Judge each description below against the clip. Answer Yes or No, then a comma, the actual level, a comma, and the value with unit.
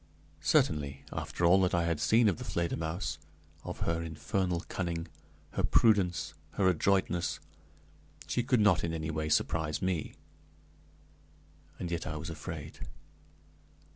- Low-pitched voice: Yes, very low, 85 Hz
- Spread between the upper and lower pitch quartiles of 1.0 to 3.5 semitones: Yes, average, 2.9 semitones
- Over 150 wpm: No, slow, 135 wpm